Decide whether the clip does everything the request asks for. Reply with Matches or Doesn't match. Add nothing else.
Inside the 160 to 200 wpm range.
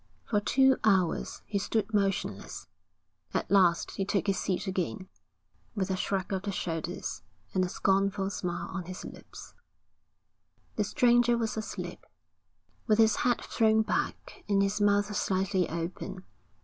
Doesn't match